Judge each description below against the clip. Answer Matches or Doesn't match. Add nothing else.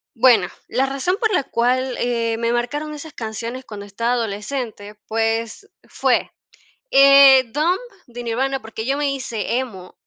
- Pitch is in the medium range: Doesn't match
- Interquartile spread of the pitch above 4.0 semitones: Doesn't match